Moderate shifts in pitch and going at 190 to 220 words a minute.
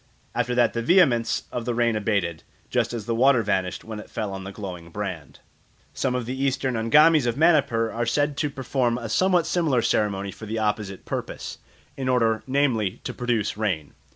Yes: average, 3.9 semitones; average, 195 wpm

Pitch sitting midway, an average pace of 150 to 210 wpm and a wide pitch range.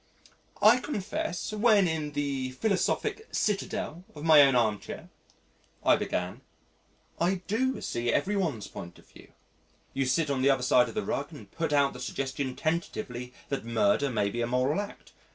Yes: medium, 145 Hz; average, 170 wpm; wide, 6.5 semitones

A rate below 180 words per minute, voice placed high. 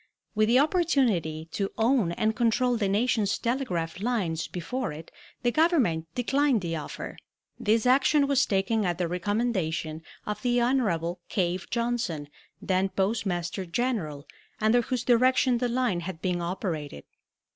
Yes: average, 140 wpm; high, 210 Hz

